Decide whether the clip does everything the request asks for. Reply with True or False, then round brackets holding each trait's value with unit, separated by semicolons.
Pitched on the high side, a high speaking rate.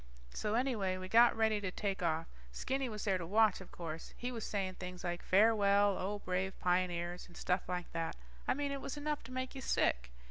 True (195 Hz; 215 wpm)